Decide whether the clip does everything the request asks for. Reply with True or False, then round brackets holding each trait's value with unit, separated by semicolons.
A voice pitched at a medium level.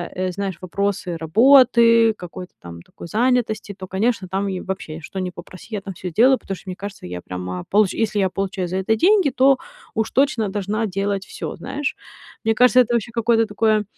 False (200 Hz)